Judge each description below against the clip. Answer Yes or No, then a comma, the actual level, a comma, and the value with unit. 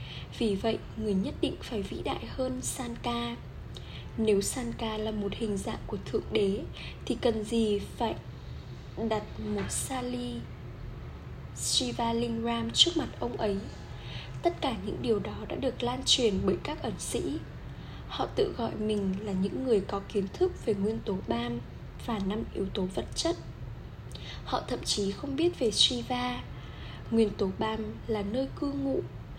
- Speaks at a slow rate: Yes, slow, 160 wpm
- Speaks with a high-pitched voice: Yes, high, 205 Hz